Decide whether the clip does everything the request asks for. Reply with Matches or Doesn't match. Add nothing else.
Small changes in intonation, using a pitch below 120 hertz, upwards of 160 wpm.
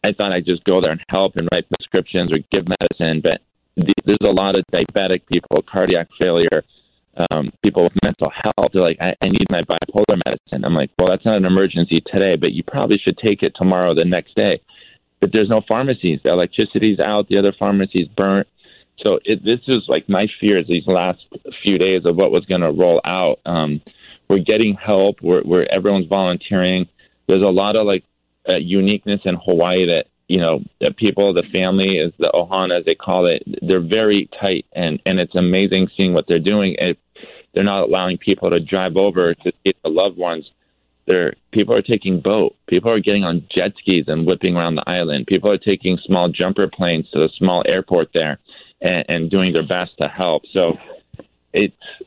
Matches